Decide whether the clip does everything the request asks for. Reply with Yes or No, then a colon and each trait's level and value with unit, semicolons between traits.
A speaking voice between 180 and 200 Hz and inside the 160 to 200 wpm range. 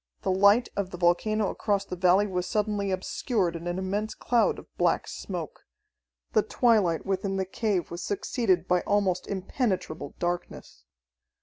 No: high, 190 Hz; average, 150 wpm